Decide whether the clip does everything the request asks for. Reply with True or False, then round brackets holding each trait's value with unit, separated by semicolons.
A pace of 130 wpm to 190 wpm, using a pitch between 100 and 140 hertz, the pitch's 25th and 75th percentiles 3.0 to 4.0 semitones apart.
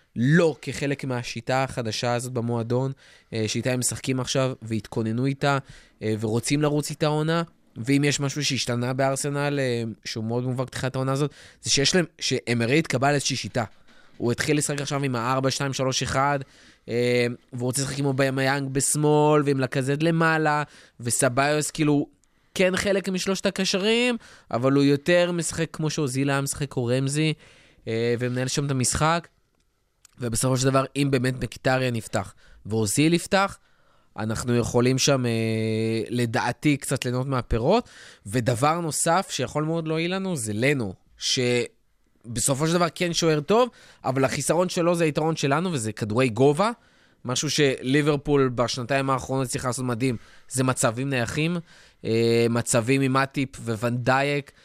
True (140 wpm; 135 Hz; 3.5 semitones)